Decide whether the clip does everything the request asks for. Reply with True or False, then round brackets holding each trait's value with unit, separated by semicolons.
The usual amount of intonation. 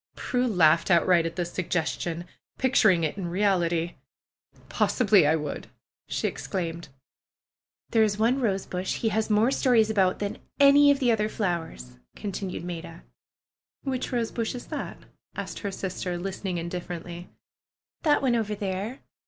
True (4.4 semitones)